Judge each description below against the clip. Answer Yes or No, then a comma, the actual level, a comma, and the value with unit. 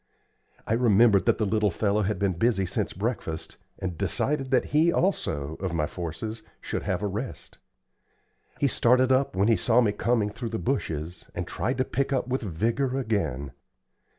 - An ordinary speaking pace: Yes, average, 175 wpm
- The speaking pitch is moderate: No, low, 110 Hz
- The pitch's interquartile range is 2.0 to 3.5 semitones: No, average, 5.1 semitones